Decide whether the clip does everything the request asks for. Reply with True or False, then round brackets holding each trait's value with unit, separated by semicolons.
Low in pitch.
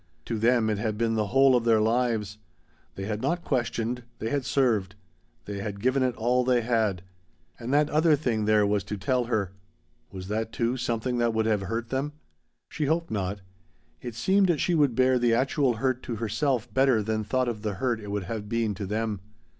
True (115 Hz)